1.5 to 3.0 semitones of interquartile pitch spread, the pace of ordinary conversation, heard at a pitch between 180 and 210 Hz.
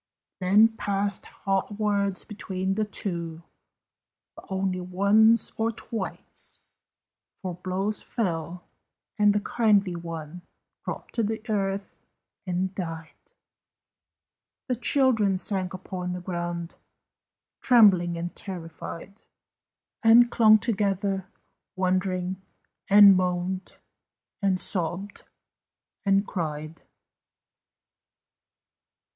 No: narrow, 2.6 semitones; slow, 90 wpm; high, 190 Hz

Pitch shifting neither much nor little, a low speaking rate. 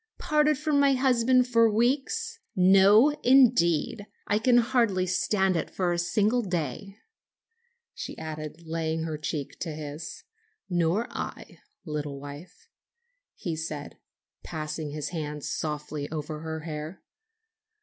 No: wide, 7.2 semitones; slow, 125 wpm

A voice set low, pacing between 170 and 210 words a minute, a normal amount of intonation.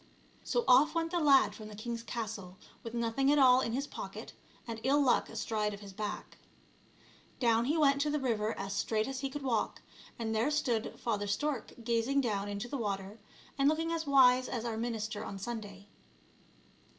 No: high, 235 Hz; average, 190 wpm; average, 4.2 semitones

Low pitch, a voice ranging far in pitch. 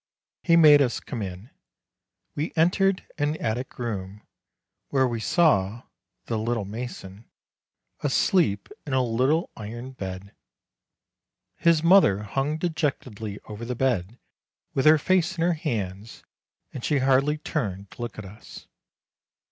Yes: low, 125 Hz; wide, 6.4 semitones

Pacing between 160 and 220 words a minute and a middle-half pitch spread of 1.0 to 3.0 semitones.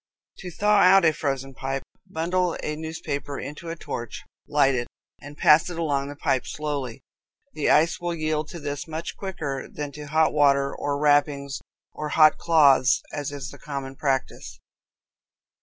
Yes: average, 165 wpm; narrow, 2.5 semitones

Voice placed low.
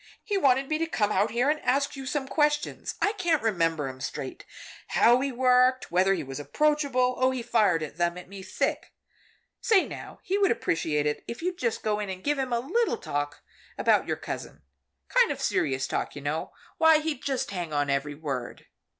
No: high, 235 Hz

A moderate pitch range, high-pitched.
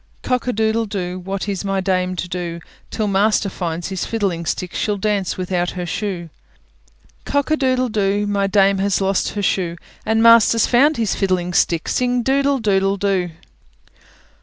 Yes: average, 3.3 semitones; high, 195 Hz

